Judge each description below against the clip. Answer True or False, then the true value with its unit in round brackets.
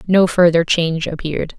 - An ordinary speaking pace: True (150 wpm)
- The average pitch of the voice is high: False (170 Hz)